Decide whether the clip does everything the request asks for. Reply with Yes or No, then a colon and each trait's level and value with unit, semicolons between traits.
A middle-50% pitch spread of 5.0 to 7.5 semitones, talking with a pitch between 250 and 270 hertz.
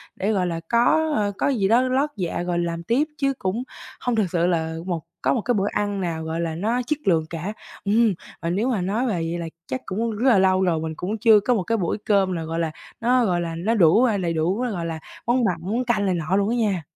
No: average, 5.3 semitones; high, 195 Hz